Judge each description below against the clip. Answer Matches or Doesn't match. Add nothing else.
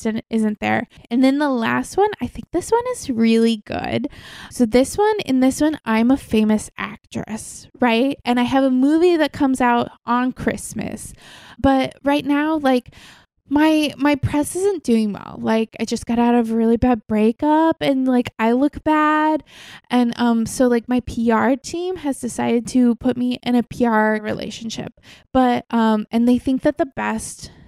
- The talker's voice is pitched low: Doesn't match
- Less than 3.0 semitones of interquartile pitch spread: Doesn't match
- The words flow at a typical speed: Matches